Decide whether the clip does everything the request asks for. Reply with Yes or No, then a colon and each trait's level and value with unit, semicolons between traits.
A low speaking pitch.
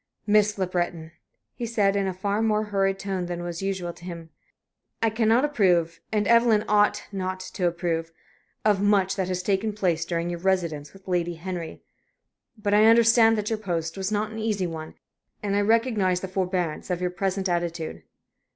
No: high, 190 Hz